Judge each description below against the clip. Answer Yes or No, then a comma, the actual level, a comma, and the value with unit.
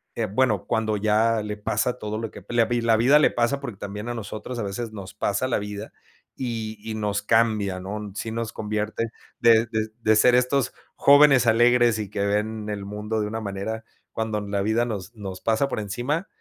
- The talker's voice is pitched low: Yes, low, 110 Hz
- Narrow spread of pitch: Yes, narrow, 2.1 semitones